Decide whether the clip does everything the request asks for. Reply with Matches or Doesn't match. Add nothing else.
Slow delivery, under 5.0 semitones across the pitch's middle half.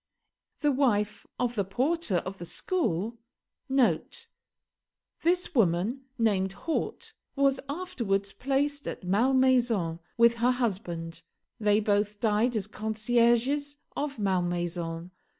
Doesn't match